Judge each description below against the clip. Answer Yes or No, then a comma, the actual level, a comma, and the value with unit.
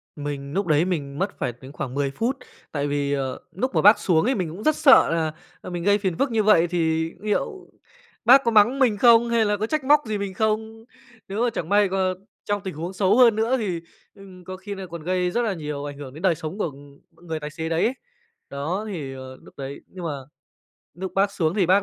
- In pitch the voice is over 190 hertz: No, medium, 185 Hz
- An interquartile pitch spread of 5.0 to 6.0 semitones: Yes, wide, 5.6 semitones